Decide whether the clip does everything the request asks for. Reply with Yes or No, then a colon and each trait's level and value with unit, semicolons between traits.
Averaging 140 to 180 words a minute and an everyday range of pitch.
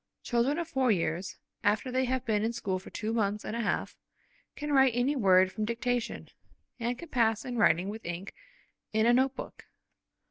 No: average, 190 wpm; average, 3.7 semitones